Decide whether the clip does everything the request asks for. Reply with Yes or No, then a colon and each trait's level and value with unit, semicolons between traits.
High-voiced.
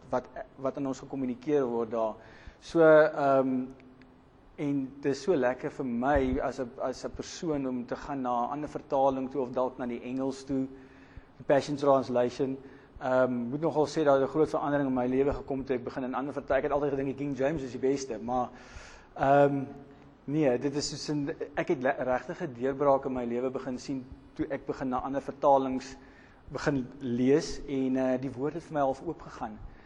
No: low, 135 Hz